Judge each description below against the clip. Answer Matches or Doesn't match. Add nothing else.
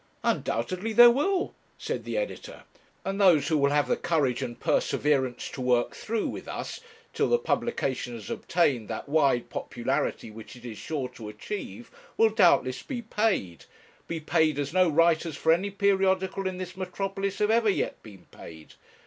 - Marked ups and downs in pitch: Matches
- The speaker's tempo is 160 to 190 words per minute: Matches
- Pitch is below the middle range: Doesn't match